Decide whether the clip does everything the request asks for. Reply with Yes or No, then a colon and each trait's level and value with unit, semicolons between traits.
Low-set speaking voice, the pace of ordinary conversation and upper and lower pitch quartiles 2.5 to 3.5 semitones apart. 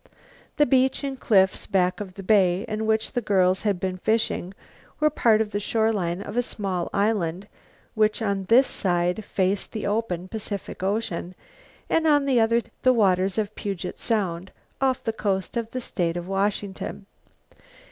No: high, 205 Hz; average, 170 wpm; average, 3.2 semitones